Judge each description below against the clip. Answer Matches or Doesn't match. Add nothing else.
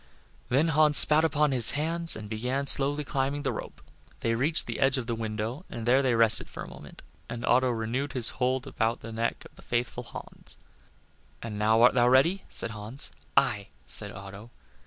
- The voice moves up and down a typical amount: Matches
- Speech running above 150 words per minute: Matches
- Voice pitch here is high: Doesn't match